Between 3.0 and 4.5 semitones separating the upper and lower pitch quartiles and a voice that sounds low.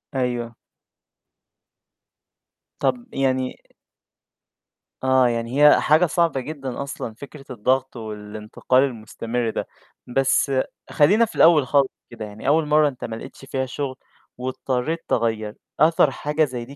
Yes: average, 3.6 semitones; low, 130 Hz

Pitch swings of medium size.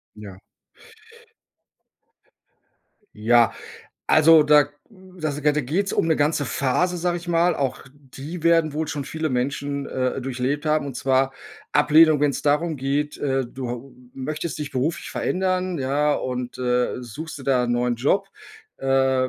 Yes: average, 3.6 semitones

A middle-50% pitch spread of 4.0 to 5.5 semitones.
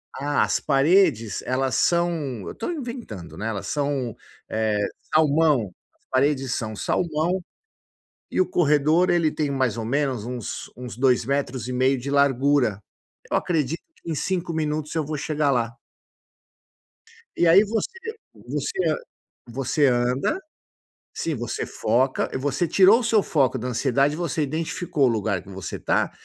Yes: average, 4.5 semitones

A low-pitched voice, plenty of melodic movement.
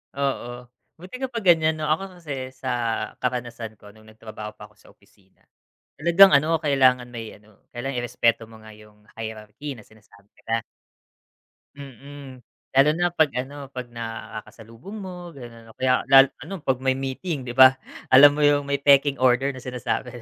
No: low, 130 Hz; average, 4.1 semitones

